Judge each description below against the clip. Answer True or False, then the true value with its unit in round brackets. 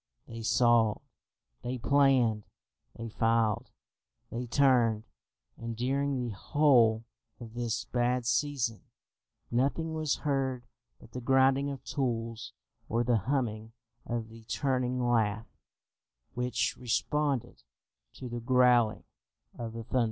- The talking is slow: True (115 wpm)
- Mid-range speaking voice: False (120 Hz)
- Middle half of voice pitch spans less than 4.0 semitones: True (2.6 semitones)